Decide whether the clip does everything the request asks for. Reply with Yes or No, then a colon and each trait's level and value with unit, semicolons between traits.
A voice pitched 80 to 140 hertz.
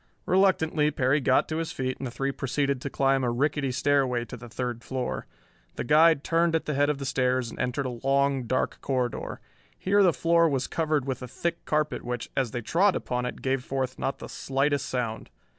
Yes: low, 135 Hz